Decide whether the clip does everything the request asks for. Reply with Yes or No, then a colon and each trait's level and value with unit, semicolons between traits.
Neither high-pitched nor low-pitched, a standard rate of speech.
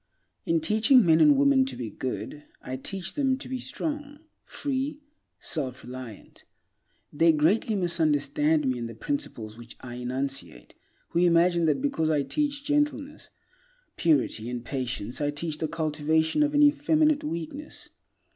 Yes: medium, 165 Hz; average, 150 wpm